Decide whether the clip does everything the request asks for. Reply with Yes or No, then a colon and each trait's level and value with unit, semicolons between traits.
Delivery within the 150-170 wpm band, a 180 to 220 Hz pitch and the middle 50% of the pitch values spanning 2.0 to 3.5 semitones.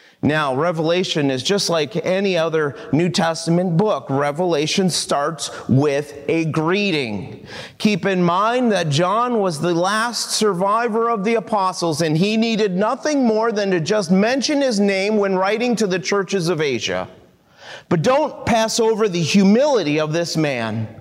No: average, 155 wpm; high, 190 Hz; average, 4.9 semitones